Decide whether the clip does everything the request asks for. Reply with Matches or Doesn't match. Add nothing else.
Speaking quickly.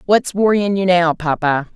Doesn't match